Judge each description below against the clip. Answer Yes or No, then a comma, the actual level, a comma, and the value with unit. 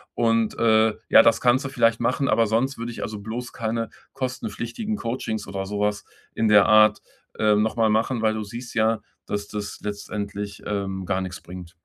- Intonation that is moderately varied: No, narrow, 2.2 semitones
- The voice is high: No, low, 110 Hz